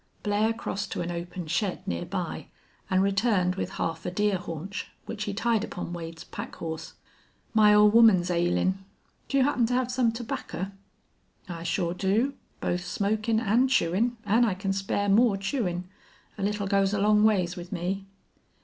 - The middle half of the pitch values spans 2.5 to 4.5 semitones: Yes, average, 3.5 semitones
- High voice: Yes, high, 200 Hz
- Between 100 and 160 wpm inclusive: No, average, 175 wpm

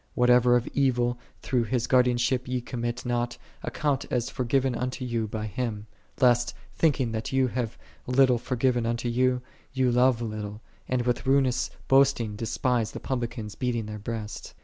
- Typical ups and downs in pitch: No, narrow, 1.7 semitones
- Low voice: Yes, low, 120 Hz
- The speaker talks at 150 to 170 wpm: Yes, average, 160 wpm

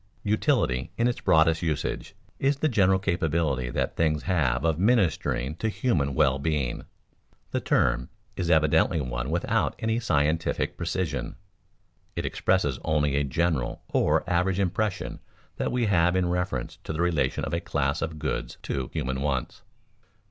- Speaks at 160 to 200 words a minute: No, average, 150 wpm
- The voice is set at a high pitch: No, very low, 80 Hz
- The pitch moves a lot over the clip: No, average, 4.8 semitones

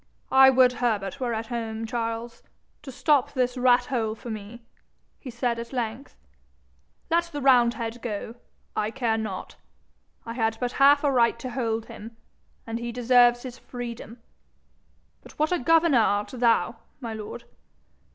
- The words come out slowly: No, average, 155 wpm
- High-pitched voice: Yes, high, 240 Hz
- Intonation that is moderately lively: No, narrow, 2.2 semitones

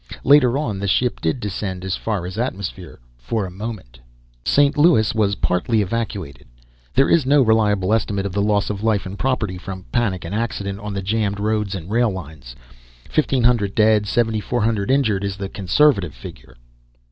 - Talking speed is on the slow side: No, average, 170 wpm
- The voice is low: Yes, low, 105 Hz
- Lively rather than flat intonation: No, average, 3.4 semitones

